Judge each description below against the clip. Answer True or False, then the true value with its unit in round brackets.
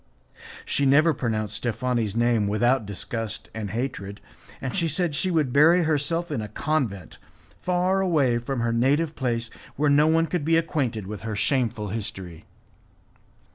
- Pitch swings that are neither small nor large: False (5.9 semitones)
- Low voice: True (125 Hz)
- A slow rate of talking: False (155 wpm)